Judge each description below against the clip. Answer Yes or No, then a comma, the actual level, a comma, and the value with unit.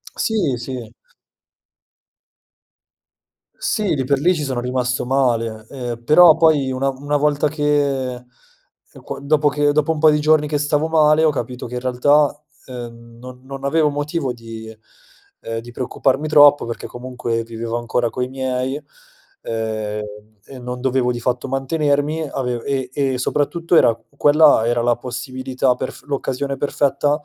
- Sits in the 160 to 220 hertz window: No, low, 135 Hz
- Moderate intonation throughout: Yes, average, 3.1 semitones